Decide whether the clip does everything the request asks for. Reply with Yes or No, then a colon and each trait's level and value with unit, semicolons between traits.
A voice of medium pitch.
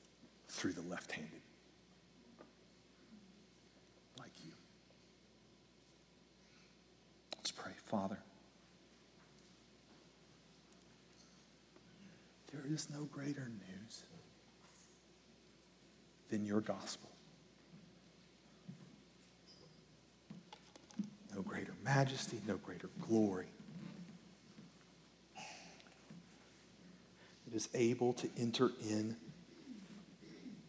Yes: medium, 180 Hz